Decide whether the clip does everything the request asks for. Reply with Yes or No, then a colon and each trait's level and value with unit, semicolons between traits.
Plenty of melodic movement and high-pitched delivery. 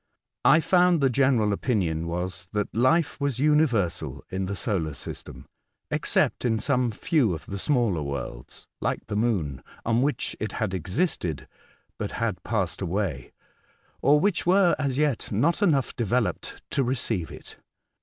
No: wide, 7.4 semitones; low, 115 Hz